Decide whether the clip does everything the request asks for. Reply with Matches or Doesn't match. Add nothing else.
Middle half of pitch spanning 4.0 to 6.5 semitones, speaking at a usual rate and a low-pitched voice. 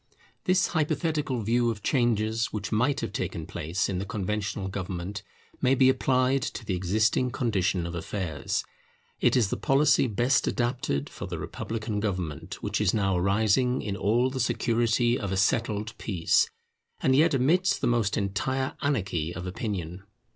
Matches